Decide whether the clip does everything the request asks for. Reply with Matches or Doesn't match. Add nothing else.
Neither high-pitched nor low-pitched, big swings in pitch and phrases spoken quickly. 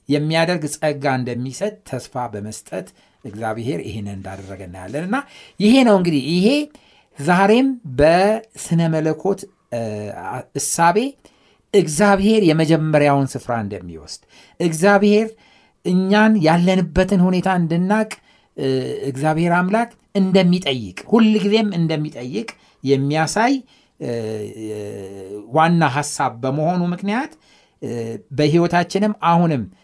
Doesn't match